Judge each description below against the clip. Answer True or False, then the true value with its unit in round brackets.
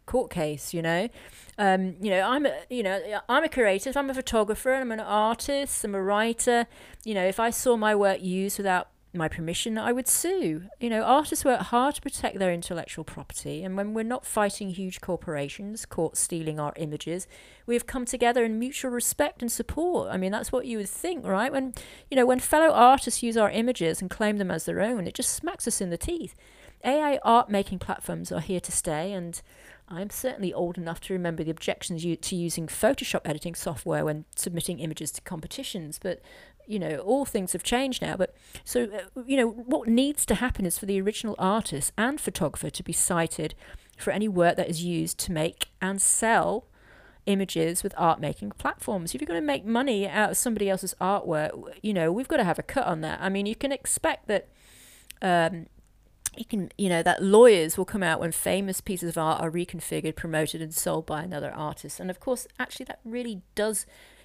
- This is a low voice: False (195 Hz)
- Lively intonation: True (5.9 semitones)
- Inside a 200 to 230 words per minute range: True (205 wpm)